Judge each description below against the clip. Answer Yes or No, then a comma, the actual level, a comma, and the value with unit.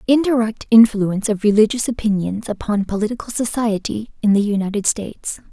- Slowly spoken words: Yes, slow, 130 wpm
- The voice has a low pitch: No, high, 215 Hz